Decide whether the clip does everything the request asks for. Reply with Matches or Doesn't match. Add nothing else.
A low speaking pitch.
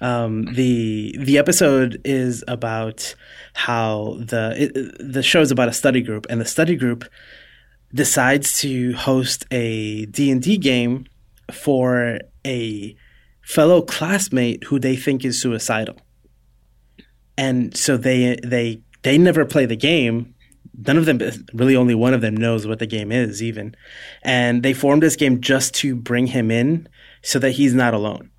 Matches